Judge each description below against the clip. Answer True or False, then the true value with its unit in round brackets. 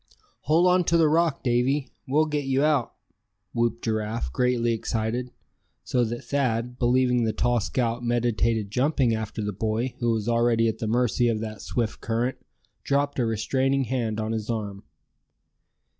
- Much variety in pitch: False (2.8 semitones)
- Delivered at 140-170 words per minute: True (160 wpm)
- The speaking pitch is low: True (120 Hz)